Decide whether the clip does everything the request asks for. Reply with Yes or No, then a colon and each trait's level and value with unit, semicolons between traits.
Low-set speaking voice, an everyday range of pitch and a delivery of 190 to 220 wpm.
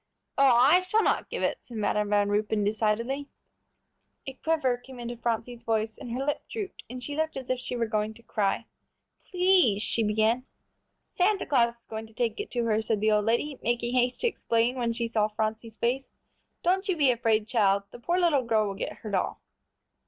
No: high, 235 Hz; average, 3.5 semitones; fast, 205 wpm